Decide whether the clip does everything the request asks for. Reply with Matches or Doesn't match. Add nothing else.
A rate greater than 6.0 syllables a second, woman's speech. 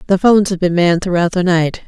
Matches